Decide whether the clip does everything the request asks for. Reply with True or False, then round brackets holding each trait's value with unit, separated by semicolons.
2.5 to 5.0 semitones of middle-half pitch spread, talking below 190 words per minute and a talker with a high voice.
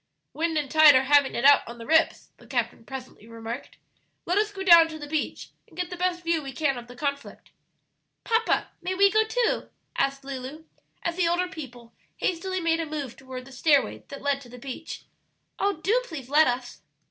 False (4.7 semitones; 205 wpm; 300 Hz)